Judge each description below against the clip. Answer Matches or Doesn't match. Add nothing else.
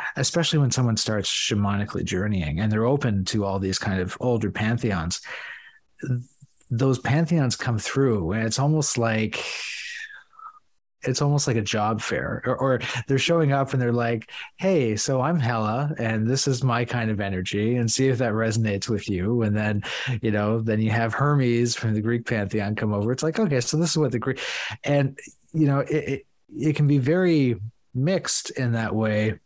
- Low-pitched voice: Matches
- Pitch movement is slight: Doesn't match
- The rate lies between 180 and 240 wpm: Matches